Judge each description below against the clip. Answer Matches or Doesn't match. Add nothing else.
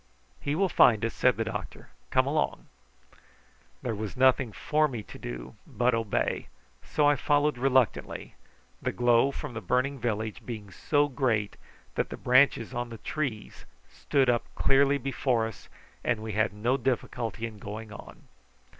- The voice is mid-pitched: Doesn't match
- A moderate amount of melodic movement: Matches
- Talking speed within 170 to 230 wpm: Doesn't match